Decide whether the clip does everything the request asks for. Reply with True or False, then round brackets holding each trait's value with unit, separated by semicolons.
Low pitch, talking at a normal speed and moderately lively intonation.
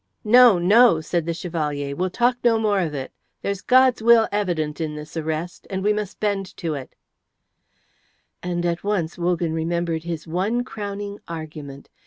False (175 Hz; 165 wpm; 4.4 semitones)